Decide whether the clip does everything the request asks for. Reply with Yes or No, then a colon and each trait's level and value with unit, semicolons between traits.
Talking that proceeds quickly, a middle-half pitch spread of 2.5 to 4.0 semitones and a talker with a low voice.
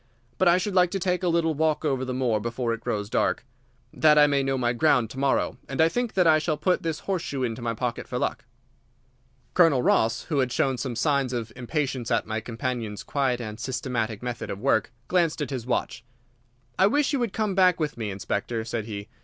No: fast, 220 wpm; wide, 5.6 semitones; low, 130 Hz